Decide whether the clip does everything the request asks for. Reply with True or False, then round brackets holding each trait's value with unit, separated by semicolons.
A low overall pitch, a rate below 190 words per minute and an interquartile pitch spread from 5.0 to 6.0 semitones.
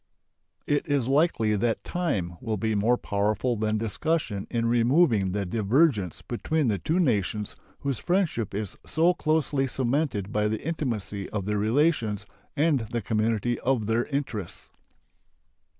True (115 Hz; 140 wpm; 5.4 semitones)